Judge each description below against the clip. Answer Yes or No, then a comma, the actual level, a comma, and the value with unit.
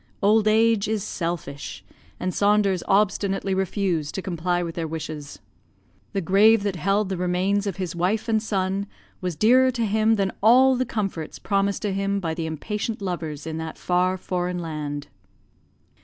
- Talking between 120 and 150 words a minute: No, average, 165 wpm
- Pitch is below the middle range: No, high, 190 Hz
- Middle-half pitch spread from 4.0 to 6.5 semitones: No, average, 3.4 semitones